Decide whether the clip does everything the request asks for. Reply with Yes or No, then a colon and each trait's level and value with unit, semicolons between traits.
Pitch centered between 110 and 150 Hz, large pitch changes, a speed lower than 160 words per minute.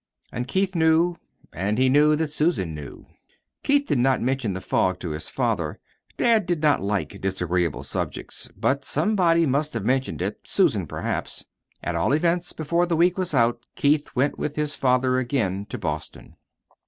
No: medium, 140 Hz; wide, 7.4 semitones; average, 170 wpm